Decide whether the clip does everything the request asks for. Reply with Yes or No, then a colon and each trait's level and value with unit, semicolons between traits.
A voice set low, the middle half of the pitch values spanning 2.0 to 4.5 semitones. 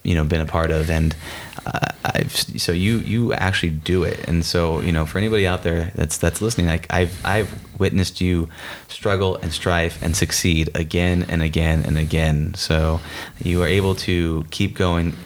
Yes: very low, 85 Hz; narrow, 2.5 semitones